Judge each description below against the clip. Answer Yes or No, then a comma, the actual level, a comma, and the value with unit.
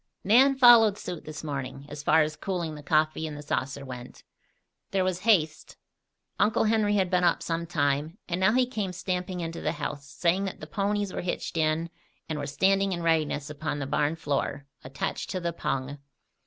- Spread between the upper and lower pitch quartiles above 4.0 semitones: Yes, average, 4.5 semitones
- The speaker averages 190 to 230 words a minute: Yes, average, 195 wpm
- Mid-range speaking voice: Yes, medium, 165 Hz